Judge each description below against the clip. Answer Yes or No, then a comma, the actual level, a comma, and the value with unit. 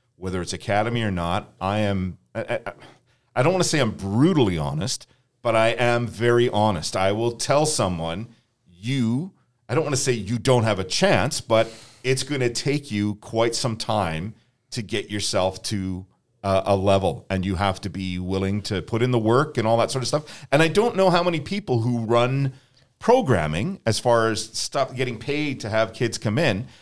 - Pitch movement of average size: Yes, average, 3.8 semitones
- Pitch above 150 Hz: No, low, 115 Hz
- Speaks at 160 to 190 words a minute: No, fast, 205 wpm